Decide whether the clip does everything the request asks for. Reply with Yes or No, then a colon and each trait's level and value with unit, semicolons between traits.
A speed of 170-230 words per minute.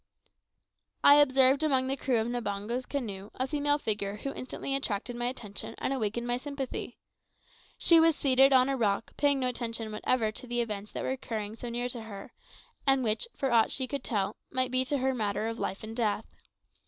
Yes: average, 200 wpm